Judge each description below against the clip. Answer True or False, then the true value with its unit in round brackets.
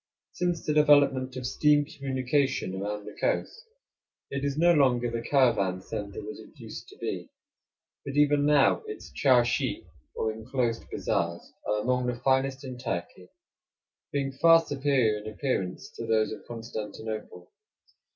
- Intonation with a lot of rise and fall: False (4.5 semitones)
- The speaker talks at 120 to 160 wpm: True (145 wpm)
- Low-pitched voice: True (130 Hz)